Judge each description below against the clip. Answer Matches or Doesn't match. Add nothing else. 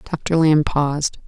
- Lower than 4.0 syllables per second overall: Matches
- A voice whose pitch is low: Doesn't match